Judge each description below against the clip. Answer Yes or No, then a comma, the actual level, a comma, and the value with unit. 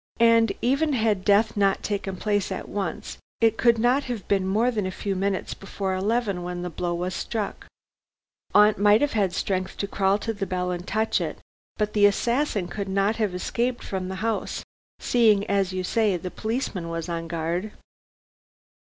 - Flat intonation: No, average, 3.1 semitones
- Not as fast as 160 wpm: No, average, 185 wpm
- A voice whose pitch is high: Yes, high, 200 Hz